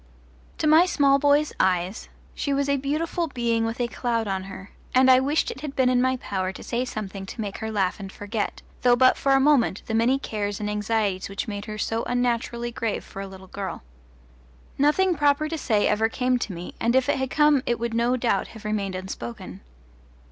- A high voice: Yes, high, 235 Hz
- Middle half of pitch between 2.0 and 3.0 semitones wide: No, average, 4.7 semitones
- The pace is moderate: No, fast, 215 wpm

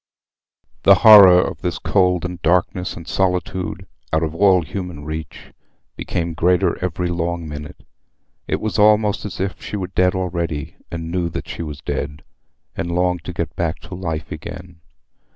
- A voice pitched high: No, very low, 90 Hz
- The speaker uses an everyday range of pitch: No, narrow, 1.9 semitones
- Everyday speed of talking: Yes, average, 155 wpm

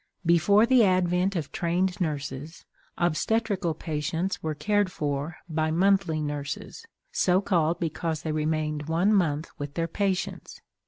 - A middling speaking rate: No, slow, 130 wpm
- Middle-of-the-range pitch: Yes, medium, 170 Hz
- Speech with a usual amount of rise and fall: Yes, average, 3.5 semitones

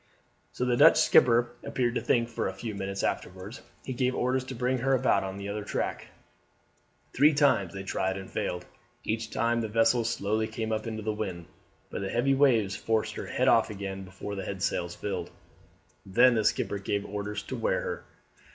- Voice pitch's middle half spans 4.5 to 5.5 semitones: No, average, 3.9 semitones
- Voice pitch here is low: Yes, low, 110 Hz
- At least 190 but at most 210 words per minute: Yes, average, 195 wpm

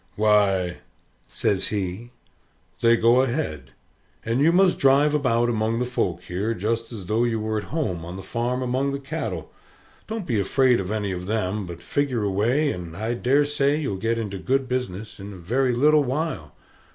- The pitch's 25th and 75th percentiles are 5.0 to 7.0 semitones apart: Yes, wide, 5.4 semitones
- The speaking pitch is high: No, low, 115 Hz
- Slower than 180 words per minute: No, average, 185 wpm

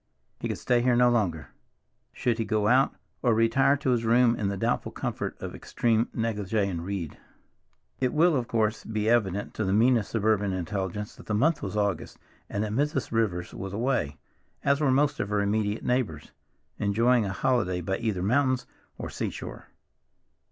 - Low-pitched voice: Yes, low, 110 Hz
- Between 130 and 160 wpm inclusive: No, average, 180 wpm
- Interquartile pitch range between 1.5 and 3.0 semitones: No, average, 3.6 semitones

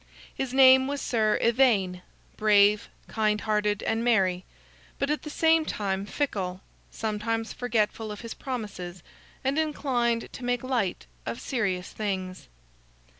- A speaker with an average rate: No, slow, 130 wpm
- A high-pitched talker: Yes, high, 220 Hz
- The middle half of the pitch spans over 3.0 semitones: Yes, average, 4.2 semitones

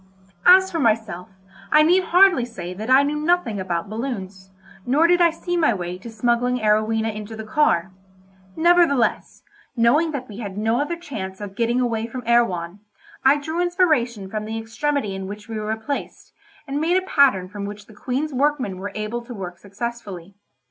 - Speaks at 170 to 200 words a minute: Yes, average, 185 wpm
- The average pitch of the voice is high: Yes, high, 230 Hz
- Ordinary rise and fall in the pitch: No, wide, 6.2 semitones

